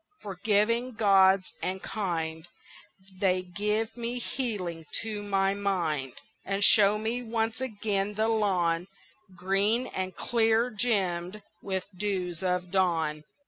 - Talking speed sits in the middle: No, slow, 115 wpm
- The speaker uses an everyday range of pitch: Yes, average, 3.3 semitones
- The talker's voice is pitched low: No, high, 195 Hz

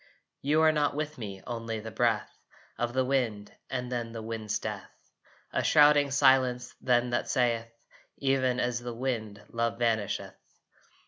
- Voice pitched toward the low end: Yes, low, 120 Hz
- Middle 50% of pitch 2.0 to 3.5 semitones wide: Yes, narrow, 2.6 semitones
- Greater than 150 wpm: No, average, 145 wpm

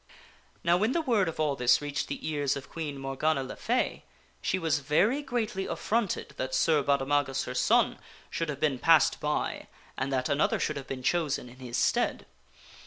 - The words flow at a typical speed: Yes, average, 180 wpm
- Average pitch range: Yes, average, 3.9 semitones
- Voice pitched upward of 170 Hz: No, medium, 150 Hz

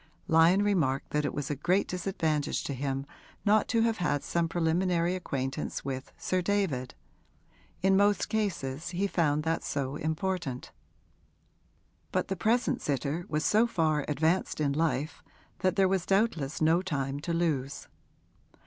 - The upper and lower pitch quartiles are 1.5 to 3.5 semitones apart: No, average, 4.6 semitones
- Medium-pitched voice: Yes, medium, 165 Hz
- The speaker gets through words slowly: No, average, 150 wpm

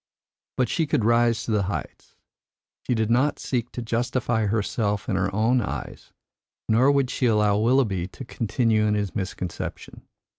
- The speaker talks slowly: No, average, 160 wpm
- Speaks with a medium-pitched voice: No, low, 115 Hz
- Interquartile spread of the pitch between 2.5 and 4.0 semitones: Yes, average, 2.9 semitones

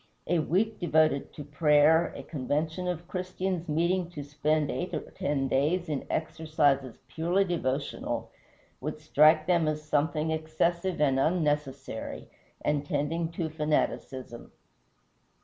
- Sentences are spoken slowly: Yes, slow, 125 wpm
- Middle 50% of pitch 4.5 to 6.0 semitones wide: No, average, 2.7 semitones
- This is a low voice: No, medium, 155 Hz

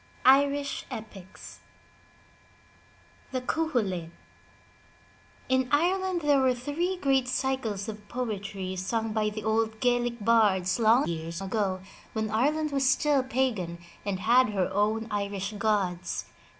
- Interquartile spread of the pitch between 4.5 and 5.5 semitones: Yes, average, 4.8 semitones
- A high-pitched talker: Yes, high, 225 Hz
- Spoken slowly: Yes, slow, 120 wpm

